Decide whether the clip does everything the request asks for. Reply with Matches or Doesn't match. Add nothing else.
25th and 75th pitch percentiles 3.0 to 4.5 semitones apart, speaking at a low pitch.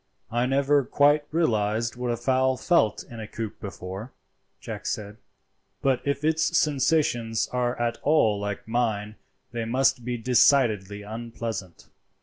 Matches